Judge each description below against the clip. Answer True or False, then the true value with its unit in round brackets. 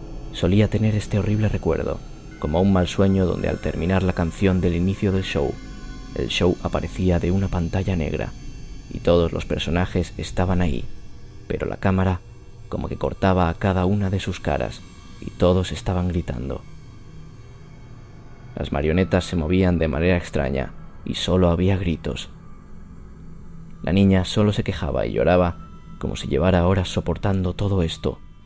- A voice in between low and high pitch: False (90 Hz)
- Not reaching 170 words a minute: True (150 wpm)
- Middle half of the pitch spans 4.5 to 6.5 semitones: False (2.9 semitones)